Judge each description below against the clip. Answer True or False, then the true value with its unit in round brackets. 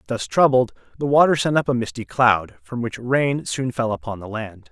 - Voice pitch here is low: True (120 Hz)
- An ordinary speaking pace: False (215 wpm)